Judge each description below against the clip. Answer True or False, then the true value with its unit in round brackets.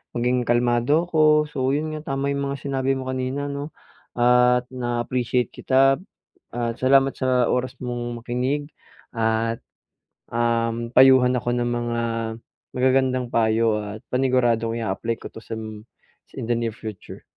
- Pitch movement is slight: True (2.2 semitones)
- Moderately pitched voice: False (125 Hz)